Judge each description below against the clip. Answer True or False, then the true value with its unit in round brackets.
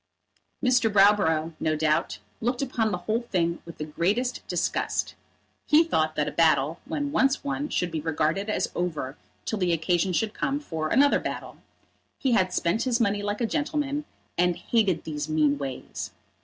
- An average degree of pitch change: False (7.4 semitones)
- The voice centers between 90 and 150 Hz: False (190 Hz)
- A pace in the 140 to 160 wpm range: False (170 wpm)